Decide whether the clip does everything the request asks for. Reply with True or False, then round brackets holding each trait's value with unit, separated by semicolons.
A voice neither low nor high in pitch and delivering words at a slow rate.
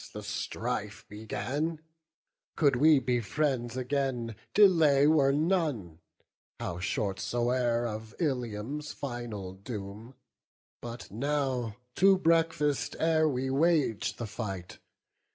False (125 Hz; 105 wpm)